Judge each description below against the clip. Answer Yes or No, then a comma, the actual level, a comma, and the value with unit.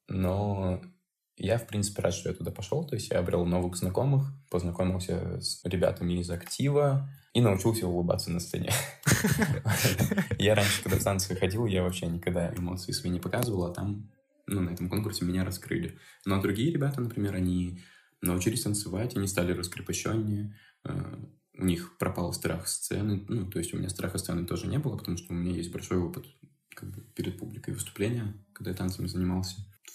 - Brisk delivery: Yes, fast, 170 wpm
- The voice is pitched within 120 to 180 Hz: No, very low, 95 Hz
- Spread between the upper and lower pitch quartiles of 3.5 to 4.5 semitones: Yes, average, 4.1 semitones